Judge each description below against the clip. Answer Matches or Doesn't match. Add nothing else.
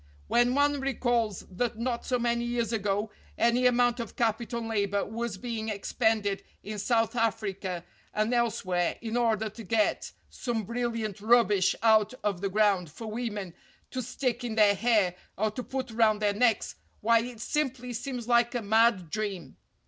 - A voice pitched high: Matches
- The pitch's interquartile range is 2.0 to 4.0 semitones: Matches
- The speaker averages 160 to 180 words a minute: Matches